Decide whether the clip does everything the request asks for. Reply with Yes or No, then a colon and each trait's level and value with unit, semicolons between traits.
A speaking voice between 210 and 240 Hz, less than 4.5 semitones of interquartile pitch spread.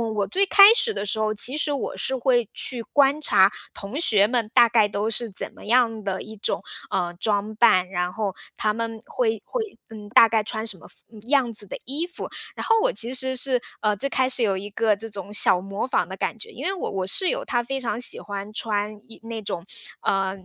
Yes: high, 225 Hz; average, 3.9 semitones